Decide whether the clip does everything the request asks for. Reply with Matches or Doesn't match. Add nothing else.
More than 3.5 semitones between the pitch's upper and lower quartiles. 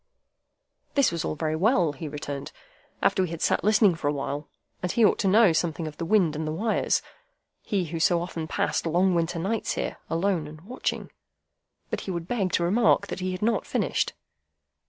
Matches